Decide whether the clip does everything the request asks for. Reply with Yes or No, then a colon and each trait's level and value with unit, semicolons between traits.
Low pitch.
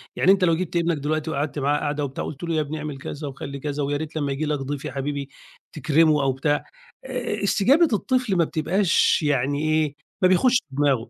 No: medium, 150 Hz